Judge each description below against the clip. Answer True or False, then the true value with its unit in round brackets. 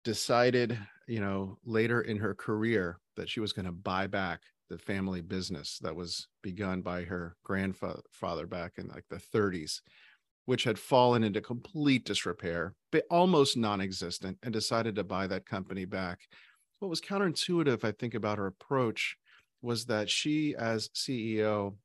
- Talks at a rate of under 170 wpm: True (155 wpm)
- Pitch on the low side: True (105 Hz)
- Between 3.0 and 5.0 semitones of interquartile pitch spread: True (4.1 semitones)